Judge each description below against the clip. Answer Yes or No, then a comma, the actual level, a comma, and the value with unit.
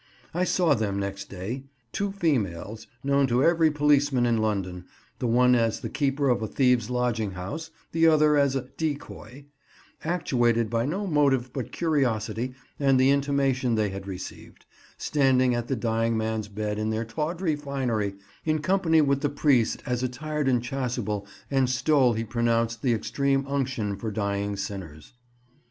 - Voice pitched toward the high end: No, low, 125 Hz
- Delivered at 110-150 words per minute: No, average, 160 wpm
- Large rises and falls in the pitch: No, average, 4.4 semitones